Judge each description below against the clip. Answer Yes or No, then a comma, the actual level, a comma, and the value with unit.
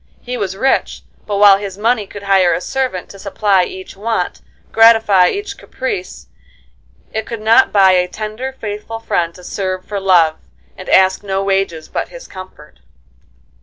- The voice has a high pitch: Yes, high, 200 Hz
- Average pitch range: Yes, average, 3.1 semitones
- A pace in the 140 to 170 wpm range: Yes, average, 165 wpm